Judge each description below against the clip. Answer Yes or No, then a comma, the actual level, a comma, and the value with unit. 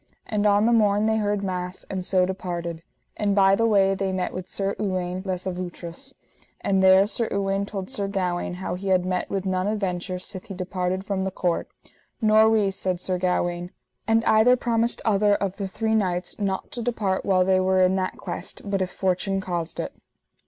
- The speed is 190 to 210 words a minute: Yes, average, 200 wpm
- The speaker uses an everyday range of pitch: No, narrow, 2.0 semitones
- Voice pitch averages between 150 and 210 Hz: Yes, high, 190 Hz